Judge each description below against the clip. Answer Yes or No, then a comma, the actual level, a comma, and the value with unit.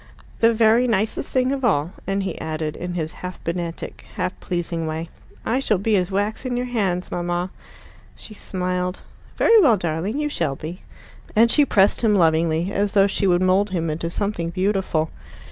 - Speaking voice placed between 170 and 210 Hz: Yes, medium, 185 Hz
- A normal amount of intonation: Yes, average, 4.1 semitones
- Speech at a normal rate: Yes, average, 180 wpm